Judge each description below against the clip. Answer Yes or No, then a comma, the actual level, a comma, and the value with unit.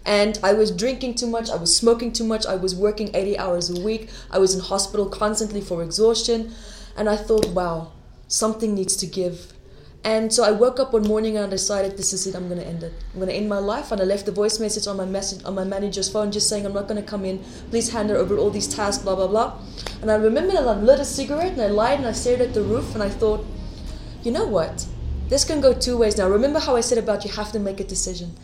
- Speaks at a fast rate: Yes, fast, 265 wpm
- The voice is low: No, high, 210 Hz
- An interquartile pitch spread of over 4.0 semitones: No, average, 2.8 semitones